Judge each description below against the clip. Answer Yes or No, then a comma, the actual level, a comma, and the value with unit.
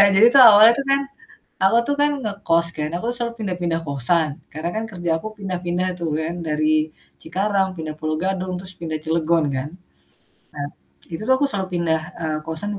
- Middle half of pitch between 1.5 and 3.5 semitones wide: No, average, 4.0 semitones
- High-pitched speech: No, medium, 175 Hz